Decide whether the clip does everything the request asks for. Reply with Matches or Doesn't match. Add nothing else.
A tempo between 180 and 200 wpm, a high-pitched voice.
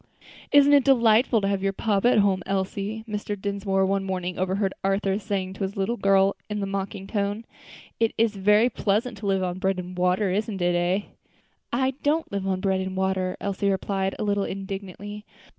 Matches